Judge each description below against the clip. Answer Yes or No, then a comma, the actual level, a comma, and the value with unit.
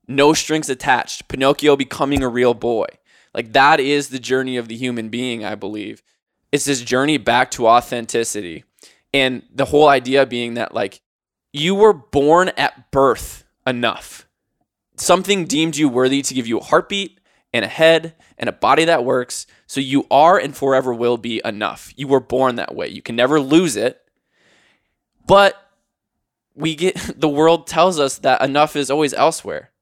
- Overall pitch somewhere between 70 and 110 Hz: No, medium, 140 Hz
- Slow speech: No, average, 170 wpm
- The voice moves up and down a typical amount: Yes, average, 3.8 semitones